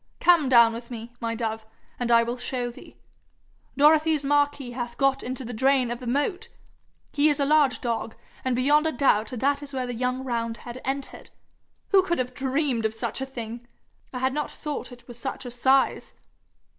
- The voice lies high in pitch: Yes, very high, 255 Hz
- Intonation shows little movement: No, average, 3.0 semitones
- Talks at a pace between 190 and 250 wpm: Yes, average, 195 wpm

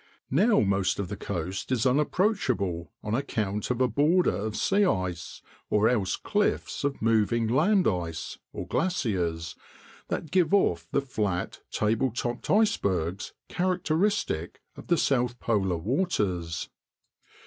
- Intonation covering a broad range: Yes, wide, 8.7 semitones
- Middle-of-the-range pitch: No, low, 115 Hz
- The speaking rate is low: Yes, slow, 125 wpm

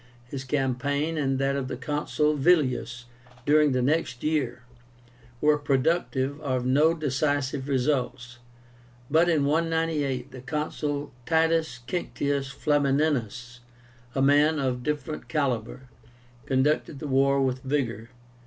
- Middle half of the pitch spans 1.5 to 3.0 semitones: Yes, narrow, 2.6 semitones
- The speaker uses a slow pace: Yes, slow, 115 wpm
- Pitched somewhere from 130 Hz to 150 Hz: Yes, medium, 140 Hz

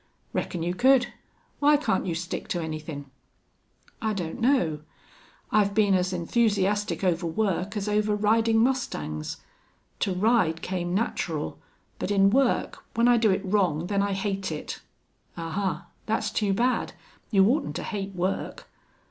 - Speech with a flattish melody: No, average, 4.0 semitones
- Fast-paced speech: No, average, 150 wpm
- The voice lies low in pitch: No, high, 195 Hz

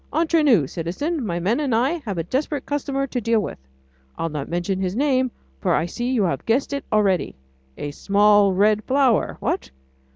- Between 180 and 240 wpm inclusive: Yes, average, 190 wpm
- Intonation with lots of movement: Yes, wide, 6.7 semitones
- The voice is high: Yes, high, 220 Hz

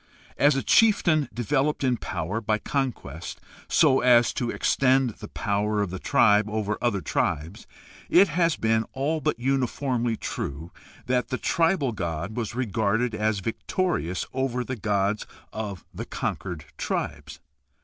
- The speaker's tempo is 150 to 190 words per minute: No, average, 140 wpm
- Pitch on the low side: Yes, low, 115 Hz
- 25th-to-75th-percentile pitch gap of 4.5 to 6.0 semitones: Yes, average, 4.8 semitones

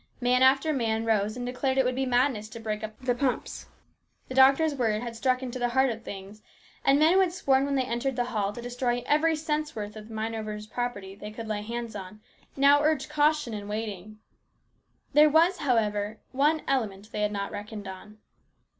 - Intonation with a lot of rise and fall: No, average, 4.2 semitones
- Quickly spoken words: Yes, fast, 210 wpm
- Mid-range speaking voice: No, high, 240 Hz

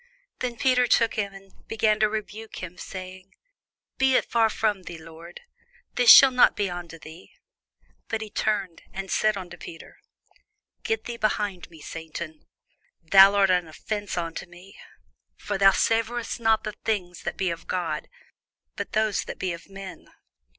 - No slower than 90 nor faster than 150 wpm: No, average, 165 wpm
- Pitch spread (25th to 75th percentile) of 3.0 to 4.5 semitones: Yes, average, 3.7 semitones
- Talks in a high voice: Yes, high, 195 Hz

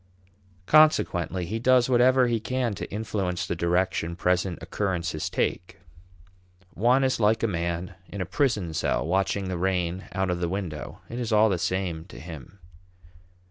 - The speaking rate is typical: Yes, average, 160 wpm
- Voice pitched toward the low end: Yes, very low, 95 Hz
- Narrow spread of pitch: No, average, 4.4 semitones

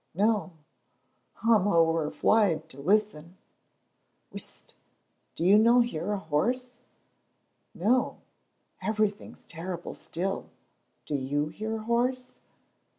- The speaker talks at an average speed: No, slow, 100 wpm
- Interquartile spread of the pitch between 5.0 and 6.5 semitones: Yes, wide, 5.4 semitones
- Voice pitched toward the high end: Yes, high, 200 Hz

